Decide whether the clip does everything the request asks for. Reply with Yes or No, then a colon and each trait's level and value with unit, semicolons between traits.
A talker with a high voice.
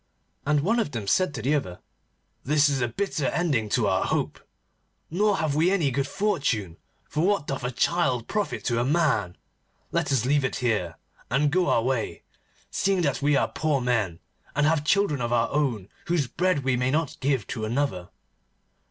No: medium, 140 Hz